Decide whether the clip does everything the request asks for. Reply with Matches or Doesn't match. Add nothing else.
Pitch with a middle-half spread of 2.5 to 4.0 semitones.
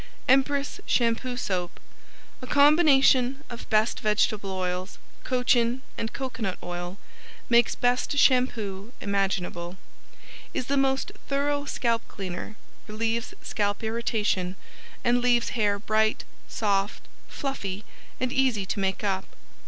Doesn't match